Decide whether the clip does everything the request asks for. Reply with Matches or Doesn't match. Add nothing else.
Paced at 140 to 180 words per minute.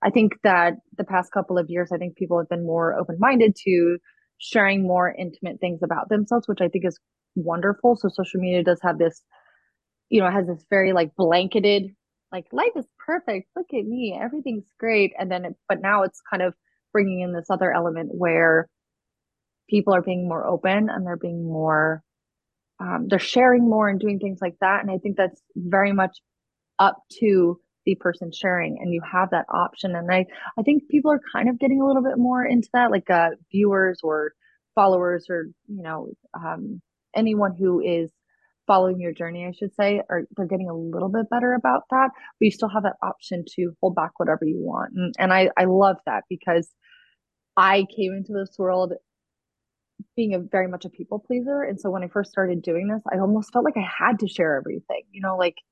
Doesn't match